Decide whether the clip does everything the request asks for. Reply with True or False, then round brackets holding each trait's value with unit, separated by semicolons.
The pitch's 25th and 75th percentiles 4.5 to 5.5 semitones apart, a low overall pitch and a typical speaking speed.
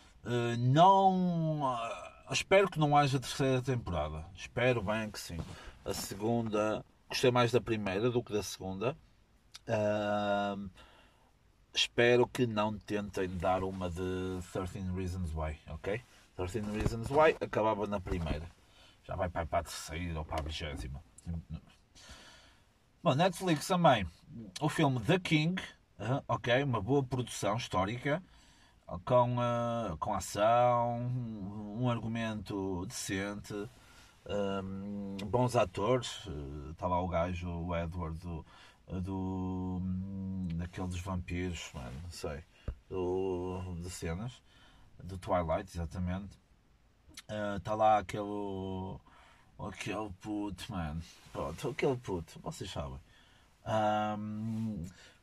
False (4.8 semitones; 100 Hz; 115 wpm)